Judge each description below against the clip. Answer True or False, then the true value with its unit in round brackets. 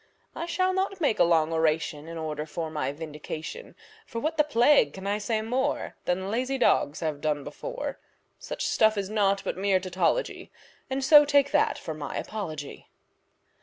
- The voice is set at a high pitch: True (200 Hz)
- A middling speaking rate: True (175 wpm)